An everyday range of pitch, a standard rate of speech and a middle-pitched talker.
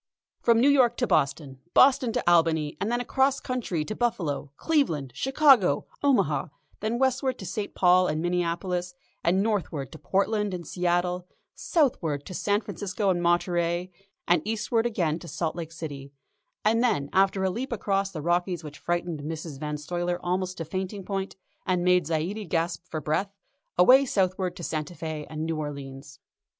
Yes: average, 4.6 semitones; average, 165 wpm; medium, 180 Hz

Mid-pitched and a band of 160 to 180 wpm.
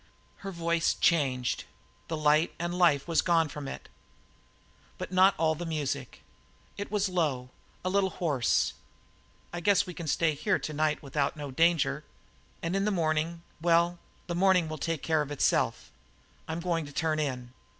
Yes: medium, 165 Hz; average, 170 wpm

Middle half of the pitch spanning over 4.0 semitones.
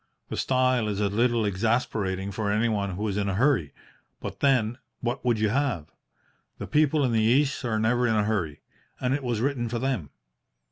No: average, 3.7 semitones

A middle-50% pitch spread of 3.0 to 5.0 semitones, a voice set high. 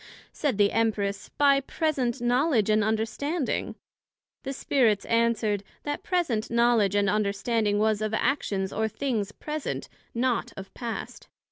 Yes: average, 4.3 semitones; high, 230 Hz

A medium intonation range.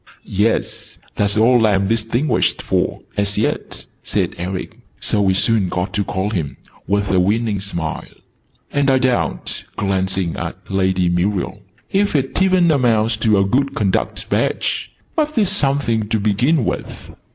Yes: average, 4.9 semitones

